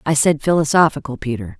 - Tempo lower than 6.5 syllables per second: Yes, 6.1 syllables/s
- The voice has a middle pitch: Yes, medium, 145 Hz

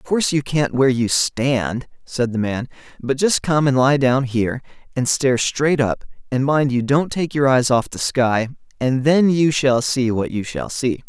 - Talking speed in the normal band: No, fast, 215 wpm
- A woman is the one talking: No, male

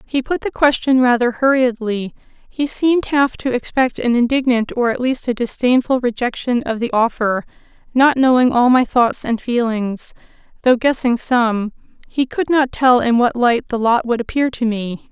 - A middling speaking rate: Yes, average, 180 wpm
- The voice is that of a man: No, female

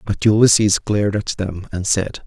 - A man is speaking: Yes, male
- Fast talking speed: No, average, 185 wpm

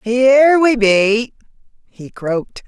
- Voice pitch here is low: No, high, 235 Hz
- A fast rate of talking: No, slow, 110 wpm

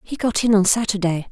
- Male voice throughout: No, female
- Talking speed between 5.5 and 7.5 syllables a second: Yes, 5.9 syllables/s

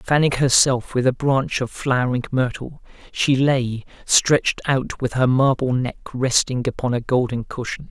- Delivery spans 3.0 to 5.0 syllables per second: Yes, 4.4 syllables/s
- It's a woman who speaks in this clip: No, male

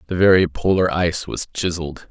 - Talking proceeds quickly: No, average, 170 wpm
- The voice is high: No, very low, 90 Hz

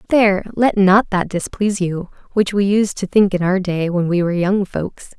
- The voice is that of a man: No, female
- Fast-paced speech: Yes, fast, 220 wpm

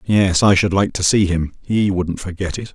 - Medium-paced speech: No, fast, 240 wpm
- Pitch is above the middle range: No, very low, 95 Hz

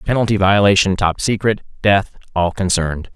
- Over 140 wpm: No, slow, 115 wpm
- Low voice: Yes, very low, 95 Hz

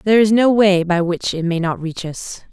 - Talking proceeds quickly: Yes, fast, 260 wpm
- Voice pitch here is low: No, high, 190 Hz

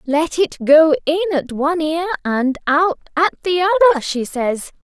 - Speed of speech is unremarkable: Yes, average, 170 wpm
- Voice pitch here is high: Yes, very high, 315 Hz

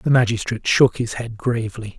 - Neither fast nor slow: Yes, average, 180 wpm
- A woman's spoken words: No, male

